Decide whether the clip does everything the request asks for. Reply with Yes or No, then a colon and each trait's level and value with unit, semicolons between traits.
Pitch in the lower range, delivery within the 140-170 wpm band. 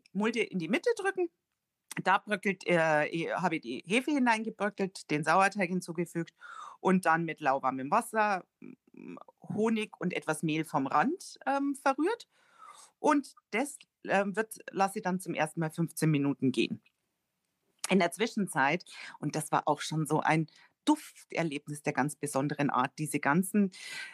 No: medium, 185 Hz; average, 150 wpm